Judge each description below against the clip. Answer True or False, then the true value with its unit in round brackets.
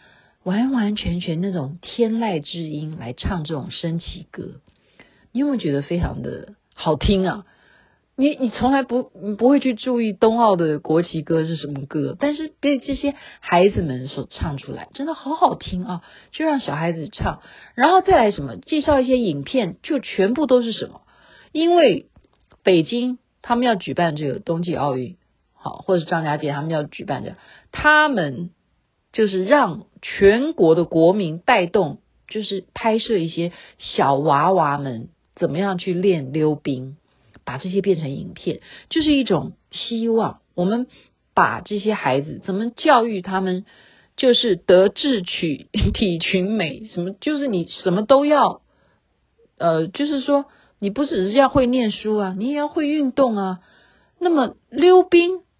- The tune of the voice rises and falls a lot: True (7.6 semitones)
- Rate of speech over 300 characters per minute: False (235 characters per minute)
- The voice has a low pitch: False (195 Hz)